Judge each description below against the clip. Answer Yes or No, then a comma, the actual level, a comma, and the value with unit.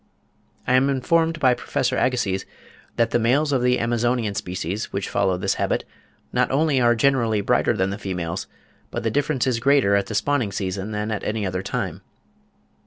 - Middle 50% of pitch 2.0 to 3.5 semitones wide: No, average, 4.8 semitones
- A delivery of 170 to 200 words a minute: Yes, average, 180 wpm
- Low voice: Yes, low, 115 Hz